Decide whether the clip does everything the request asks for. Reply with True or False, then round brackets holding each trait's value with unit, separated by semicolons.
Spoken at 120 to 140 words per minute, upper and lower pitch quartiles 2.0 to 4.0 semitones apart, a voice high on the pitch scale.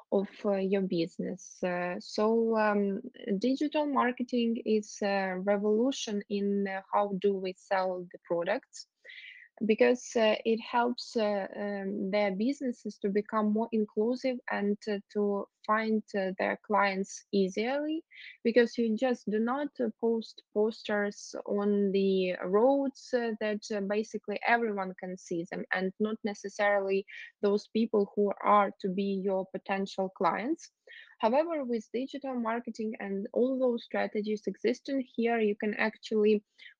True (135 wpm; 2.9 semitones; 215 Hz)